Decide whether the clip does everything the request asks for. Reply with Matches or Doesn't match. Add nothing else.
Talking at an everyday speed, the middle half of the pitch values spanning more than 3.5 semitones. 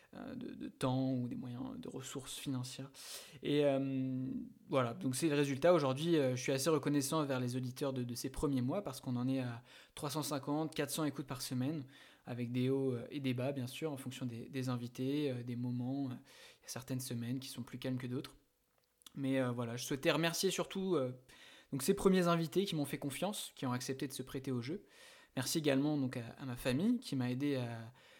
Doesn't match